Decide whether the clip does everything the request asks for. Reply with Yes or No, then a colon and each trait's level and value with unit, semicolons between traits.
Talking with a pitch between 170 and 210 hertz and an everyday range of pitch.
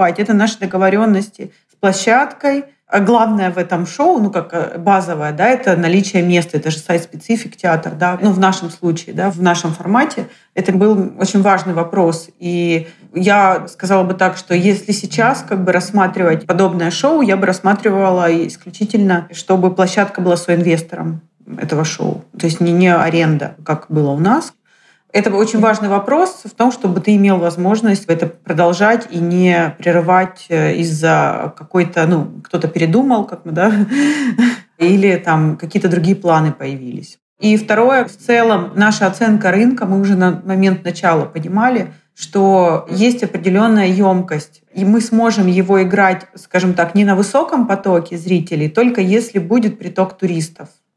Yes: high, 190 Hz; average, 3.3 semitones